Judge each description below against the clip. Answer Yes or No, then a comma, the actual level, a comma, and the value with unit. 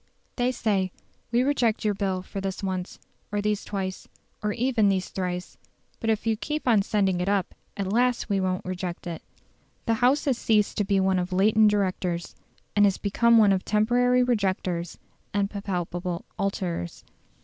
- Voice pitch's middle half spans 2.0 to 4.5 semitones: Yes, average, 3.0 semitones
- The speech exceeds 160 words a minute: Yes, average, 170 wpm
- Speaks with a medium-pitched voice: No, high, 200 Hz